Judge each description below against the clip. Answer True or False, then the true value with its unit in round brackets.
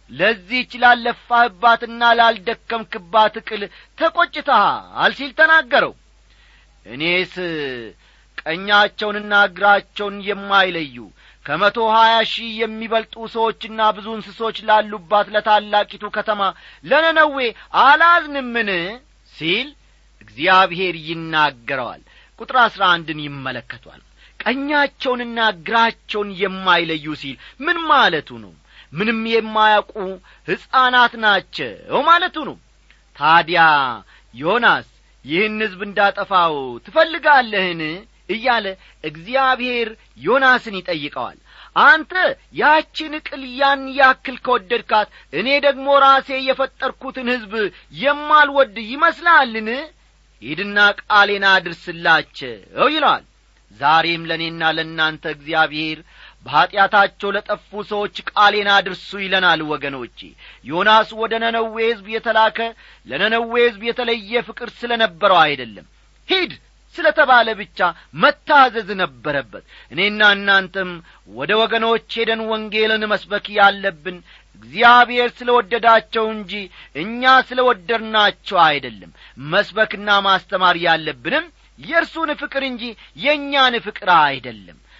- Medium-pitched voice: False (220 Hz)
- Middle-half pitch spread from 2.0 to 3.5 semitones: False (4.6 semitones)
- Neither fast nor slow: True (90 wpm)